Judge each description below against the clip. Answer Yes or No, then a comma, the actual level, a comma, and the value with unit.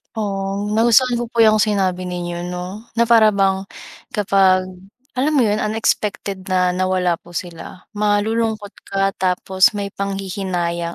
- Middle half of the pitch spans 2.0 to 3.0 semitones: Yes, average, 2.7 semitones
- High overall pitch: Yes, high, 195 Hz